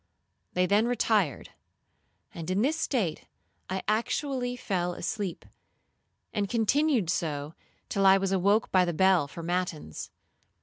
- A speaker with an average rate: No, slow, 130 wpm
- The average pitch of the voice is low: No, high, 190 Hz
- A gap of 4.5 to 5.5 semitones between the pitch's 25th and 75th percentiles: No, average, 4.1 semitones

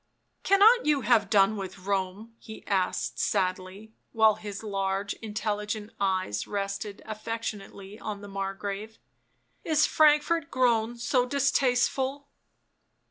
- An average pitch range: Yes, average, 3.2 semitones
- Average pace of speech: No, slow, 125 wpm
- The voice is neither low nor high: No, high, 215 Hz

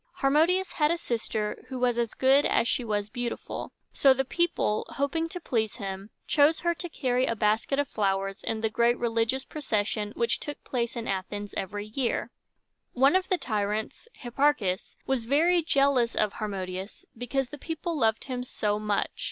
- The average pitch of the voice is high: Yes, high, 240 Hz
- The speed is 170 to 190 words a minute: Yes, average, 175 wpm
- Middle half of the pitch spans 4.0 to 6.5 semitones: Yes, average, 4.9 semitones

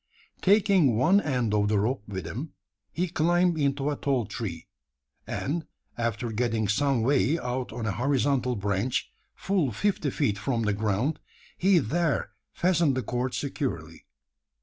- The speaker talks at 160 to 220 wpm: No, average, 150 wpm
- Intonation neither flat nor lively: No, wide, 5.8 semitones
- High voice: No, low, 130 Hz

